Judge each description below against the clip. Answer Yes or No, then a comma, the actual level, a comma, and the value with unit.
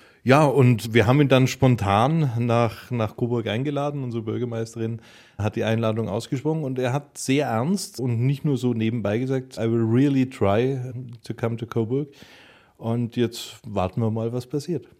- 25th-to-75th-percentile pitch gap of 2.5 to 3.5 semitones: Yes, average, 2.8 semitones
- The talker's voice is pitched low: Yes, low, 120 Hz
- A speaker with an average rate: Yes, average, 170 wpm